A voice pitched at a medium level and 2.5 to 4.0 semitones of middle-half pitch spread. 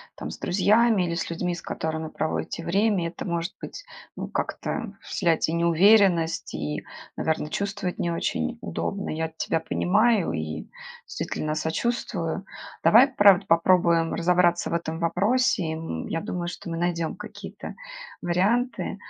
Yes: medium, 170 Hz; average, 3.5 semitones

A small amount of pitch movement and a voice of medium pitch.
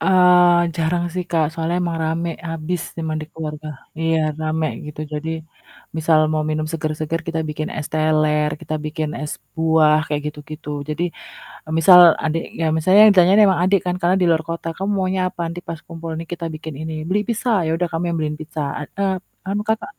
Yes: narrow, 2.3 semitones; medium, 160 Hz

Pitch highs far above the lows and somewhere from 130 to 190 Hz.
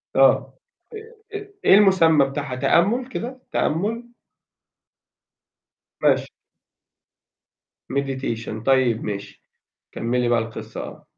Yes: wide, 9.0 semitones; medium, 140 Hz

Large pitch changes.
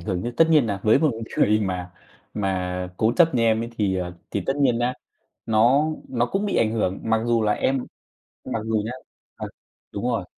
No: average, 3.6 semitones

